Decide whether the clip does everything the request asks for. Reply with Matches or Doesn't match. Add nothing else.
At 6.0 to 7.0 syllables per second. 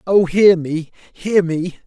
Doesn't match